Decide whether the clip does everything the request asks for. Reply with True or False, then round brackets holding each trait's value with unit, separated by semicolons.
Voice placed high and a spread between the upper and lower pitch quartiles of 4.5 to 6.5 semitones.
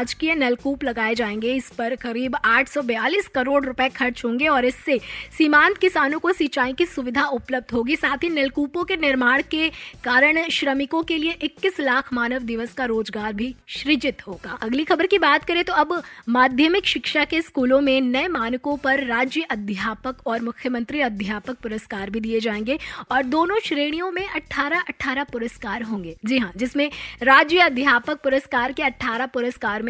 False (265 Hz; 4.0 semitones)